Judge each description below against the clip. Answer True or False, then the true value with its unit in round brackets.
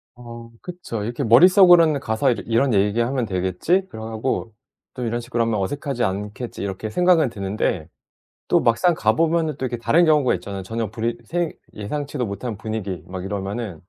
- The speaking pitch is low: True (115 Hz)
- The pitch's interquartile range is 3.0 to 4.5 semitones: False (5.5 semitones)